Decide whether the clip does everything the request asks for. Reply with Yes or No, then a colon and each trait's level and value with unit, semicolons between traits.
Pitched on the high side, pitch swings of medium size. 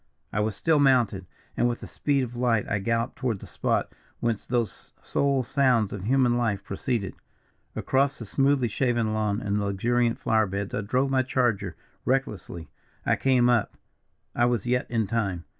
No: low, 120 Hz; average, 3.7 semitones